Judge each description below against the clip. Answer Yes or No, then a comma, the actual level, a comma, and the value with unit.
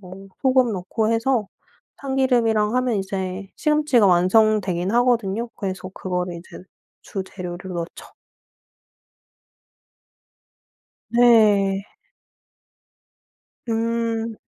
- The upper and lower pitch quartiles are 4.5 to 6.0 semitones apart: No, average, 3.8 semitones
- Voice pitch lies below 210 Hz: No, high, 215 Hz